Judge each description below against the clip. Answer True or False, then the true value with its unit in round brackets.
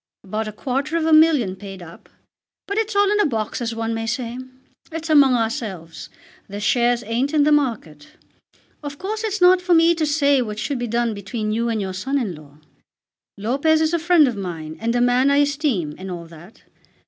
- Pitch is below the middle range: False (245 Hz)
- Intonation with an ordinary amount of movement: False (6.5 semitones)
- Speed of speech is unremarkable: False (210 wpm)